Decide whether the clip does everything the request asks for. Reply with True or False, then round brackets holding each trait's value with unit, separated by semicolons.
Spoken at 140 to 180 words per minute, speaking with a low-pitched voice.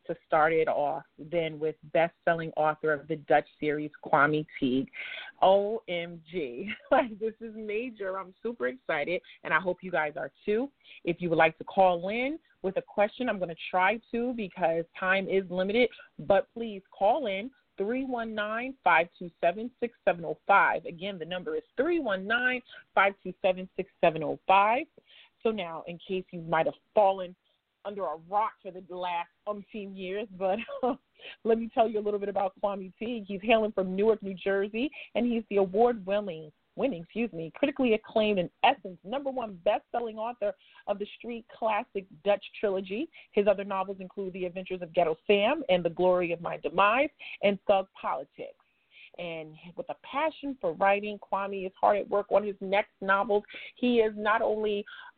False (165 wpm; 200 Hz)